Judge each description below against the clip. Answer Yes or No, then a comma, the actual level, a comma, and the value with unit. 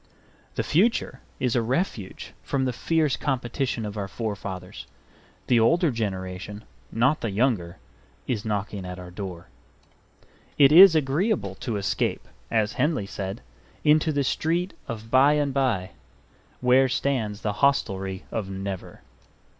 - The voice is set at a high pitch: No, low, 115 Hz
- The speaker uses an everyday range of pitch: No, wide, 5.9 semitones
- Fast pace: No, slow, 135 wpm